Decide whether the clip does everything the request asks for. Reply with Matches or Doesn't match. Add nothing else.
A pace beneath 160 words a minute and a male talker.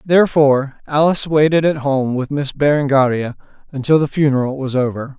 Matches